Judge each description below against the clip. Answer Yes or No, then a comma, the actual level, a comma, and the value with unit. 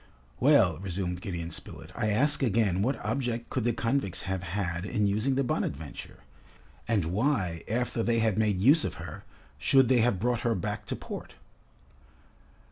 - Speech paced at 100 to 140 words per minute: No, average, 165 wpm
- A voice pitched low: Yes, low, 110 Hz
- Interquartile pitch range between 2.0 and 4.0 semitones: No, average, 4.8 semitones